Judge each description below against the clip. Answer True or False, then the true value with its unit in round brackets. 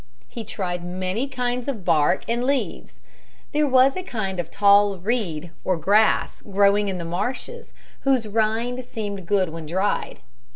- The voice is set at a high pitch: True (205 Hz)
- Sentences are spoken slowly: False (155 wpm)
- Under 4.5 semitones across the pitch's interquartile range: False (4.9 semitones)